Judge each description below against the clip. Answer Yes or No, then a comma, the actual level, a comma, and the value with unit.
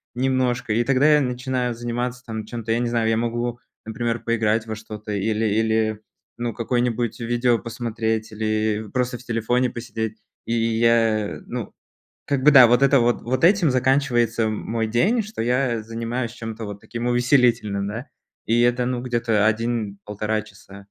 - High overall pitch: No, low, 115 Hz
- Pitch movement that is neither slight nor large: No, narrow, 2.0 semitones